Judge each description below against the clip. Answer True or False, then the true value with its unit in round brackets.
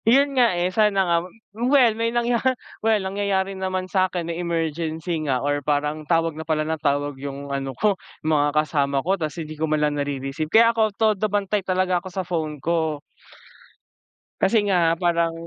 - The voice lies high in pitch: False (170 Hz)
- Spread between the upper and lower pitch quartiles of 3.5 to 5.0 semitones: True (4.6 semitones)